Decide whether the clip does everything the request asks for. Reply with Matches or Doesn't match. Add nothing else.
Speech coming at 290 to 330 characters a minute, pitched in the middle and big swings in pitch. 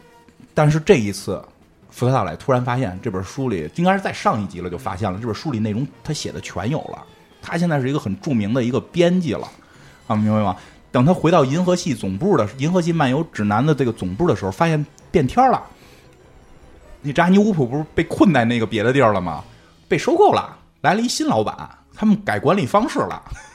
Doesn't match